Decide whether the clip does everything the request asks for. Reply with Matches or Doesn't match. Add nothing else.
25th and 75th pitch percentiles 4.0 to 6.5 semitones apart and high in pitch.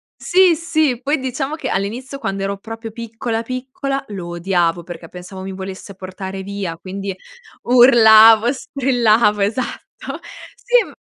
Matches